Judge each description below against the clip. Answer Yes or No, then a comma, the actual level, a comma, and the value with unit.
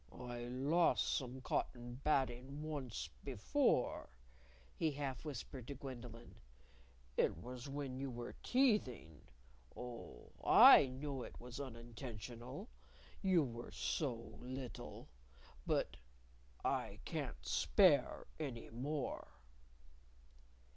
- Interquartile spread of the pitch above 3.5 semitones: No, average, 3.0 semitones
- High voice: No, low, 130 Hz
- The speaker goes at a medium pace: No, slow, 100 wpm